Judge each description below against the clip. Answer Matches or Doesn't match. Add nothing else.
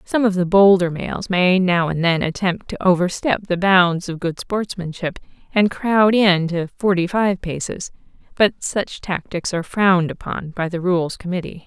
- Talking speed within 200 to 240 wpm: Doesn't match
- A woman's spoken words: Matches